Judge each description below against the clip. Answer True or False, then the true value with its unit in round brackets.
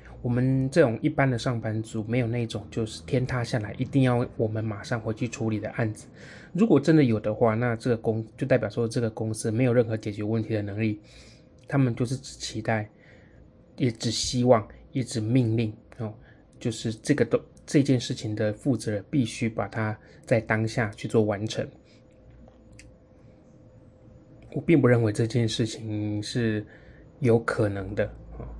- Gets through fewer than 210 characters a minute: False (250 characters per minute)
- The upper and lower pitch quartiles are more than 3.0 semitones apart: False (2.7 semitones)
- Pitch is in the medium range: False (115 Hz)